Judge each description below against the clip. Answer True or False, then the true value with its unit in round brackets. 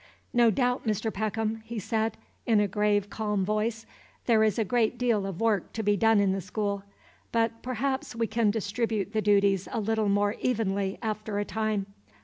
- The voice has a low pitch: False (215 Hz)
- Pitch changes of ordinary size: False (1.8 semitones)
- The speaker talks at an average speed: True (185 wpm)